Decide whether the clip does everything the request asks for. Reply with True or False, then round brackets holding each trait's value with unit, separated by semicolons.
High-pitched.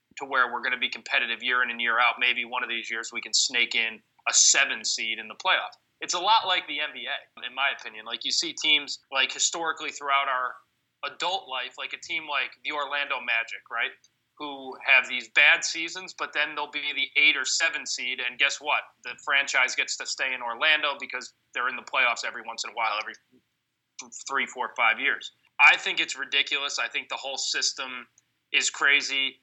False (140 Hz)